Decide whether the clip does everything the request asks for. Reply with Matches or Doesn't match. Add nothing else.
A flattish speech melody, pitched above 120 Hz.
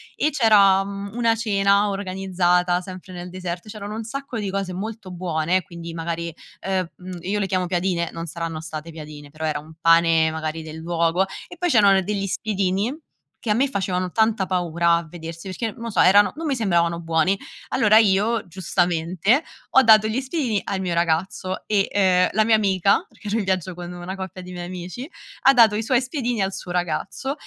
Doesn't match